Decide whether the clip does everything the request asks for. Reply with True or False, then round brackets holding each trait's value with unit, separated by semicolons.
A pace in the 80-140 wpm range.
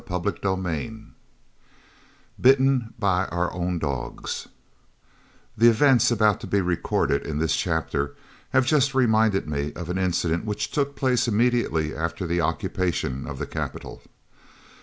True (135 wpm)